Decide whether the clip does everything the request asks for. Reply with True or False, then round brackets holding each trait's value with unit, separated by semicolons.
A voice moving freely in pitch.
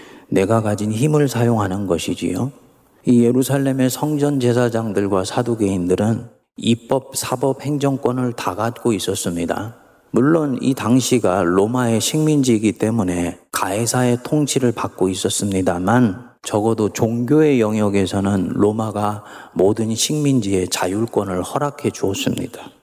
False (4.3 semitones)